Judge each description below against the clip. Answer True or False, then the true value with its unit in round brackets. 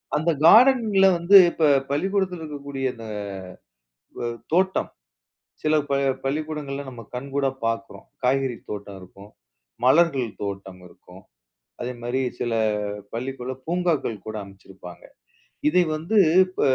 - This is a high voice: False (135 Hz)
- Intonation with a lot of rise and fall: True (6.4 semitones)